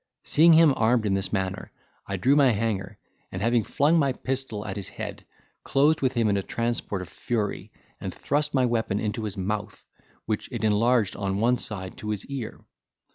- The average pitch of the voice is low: Yes, low, 110 Hz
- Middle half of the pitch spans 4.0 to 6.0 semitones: Yes, average, 4.6 semitones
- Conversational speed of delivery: Yes, average, 190 wpm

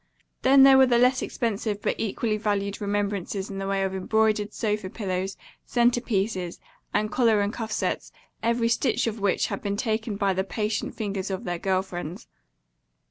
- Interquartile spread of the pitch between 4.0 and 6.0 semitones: No, average, 2.7 semitones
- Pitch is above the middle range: Yes, high, 210 Hz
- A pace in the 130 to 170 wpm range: No, average, 180 wpm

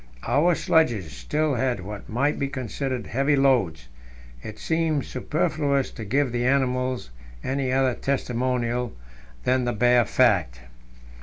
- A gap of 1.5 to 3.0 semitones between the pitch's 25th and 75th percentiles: Yes, average, 2.7 semitones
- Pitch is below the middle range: Yes, low, 130 Hz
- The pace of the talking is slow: Yes, slow, 130 wpm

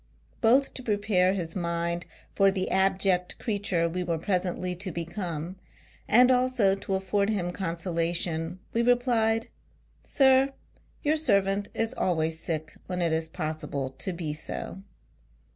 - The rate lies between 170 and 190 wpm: No, average, 145 wpm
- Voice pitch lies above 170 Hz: Yes, medium, 185 Hz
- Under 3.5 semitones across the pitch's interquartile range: No, average, 3.9 semitones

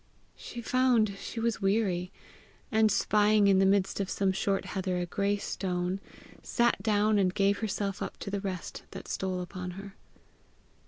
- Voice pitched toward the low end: No, high, 200 Hz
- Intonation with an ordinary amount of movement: No, narrow, 2.1 semitones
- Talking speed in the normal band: Yes, average, 165 wpm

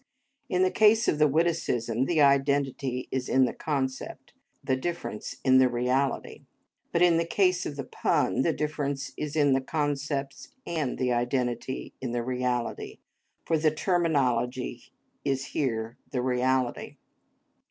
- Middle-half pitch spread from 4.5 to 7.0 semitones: No, average, 3.4 semitones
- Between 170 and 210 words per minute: No, average, 145 wpm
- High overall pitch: No, low, 135 Hz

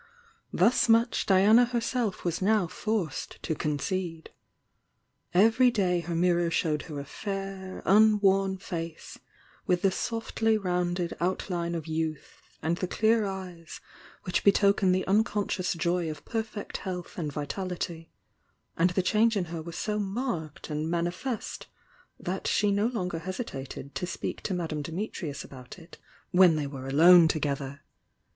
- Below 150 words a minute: Yes, average, 140 wpm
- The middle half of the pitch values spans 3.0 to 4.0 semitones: Yes, average, 3.7 semitones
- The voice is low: No, medium, 180 Hz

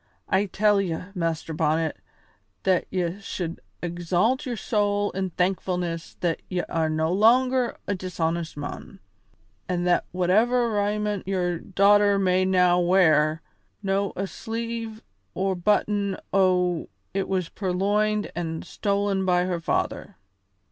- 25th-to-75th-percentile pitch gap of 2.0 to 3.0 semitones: Yes, average, 2.7 semitones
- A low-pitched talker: No, medium, 185 Hz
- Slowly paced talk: Yes, slow, 125 wpm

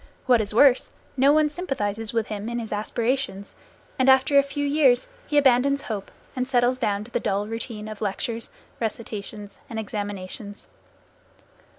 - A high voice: Yes, high, 230 Hz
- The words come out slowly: No, average, 160 wpm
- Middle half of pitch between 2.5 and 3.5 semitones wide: No, average, 4.0 semitones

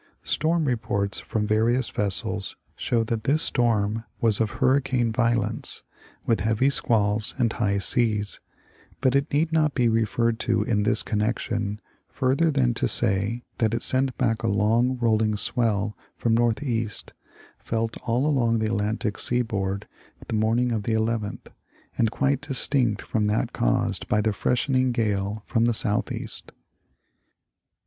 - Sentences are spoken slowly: No, average, 145 wpm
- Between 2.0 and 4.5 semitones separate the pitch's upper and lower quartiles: Yes, average, 2.7 semitones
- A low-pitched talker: Yes, low, 115 Hz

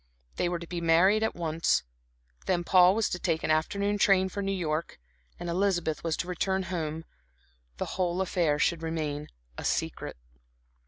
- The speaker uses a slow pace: No, average, 165 wpm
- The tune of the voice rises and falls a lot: No, narrow, 2.6 semitones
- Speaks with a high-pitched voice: No, medium, 175 Hz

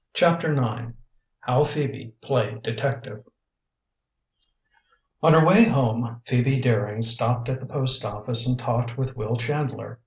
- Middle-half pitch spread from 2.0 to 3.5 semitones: Yes, average, 2.9 semitones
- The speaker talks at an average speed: No, slow, 130 wpm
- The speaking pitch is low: Yes, low, 125 Hz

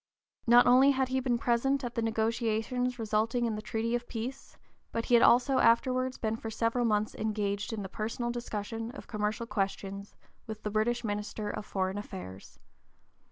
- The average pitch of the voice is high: Yes, high, 225 Hz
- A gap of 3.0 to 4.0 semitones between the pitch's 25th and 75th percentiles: No, narrow, 2.4 semitones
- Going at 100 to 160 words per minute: No, average, 185 wpm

